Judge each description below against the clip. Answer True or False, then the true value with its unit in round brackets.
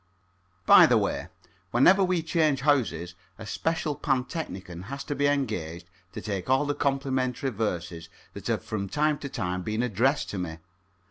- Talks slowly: False (160 wpm)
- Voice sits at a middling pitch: False (130 Hz)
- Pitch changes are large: True (7.6 semitones)